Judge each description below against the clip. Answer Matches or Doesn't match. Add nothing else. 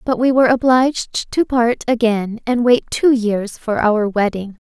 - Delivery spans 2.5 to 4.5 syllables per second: Matches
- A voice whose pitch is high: Matches